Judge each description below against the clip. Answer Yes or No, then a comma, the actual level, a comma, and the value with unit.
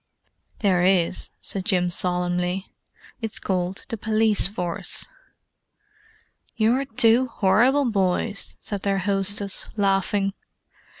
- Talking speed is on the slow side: Yes, slow, 100 wpm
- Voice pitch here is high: Yes, high, 195 Hz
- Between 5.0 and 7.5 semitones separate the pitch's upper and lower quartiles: No, average, 3.1 semitones